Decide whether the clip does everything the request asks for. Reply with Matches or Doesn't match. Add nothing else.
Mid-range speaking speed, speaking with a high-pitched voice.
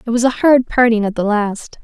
Doesn't match